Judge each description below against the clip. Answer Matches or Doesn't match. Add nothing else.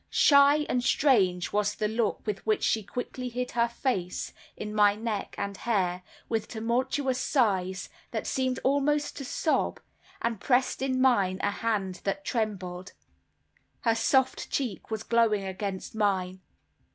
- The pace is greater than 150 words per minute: Doesn't match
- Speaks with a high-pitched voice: Matches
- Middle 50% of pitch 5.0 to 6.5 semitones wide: Doesn't match